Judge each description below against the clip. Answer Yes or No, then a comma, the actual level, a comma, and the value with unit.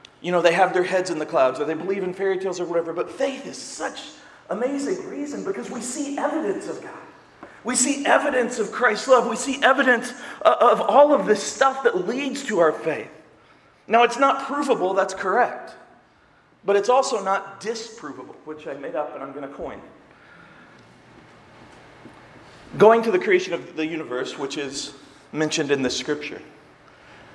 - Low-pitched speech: No, high, 225 Hz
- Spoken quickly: No, average, 180 wpm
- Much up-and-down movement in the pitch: Yes, wide, 7.5 semitones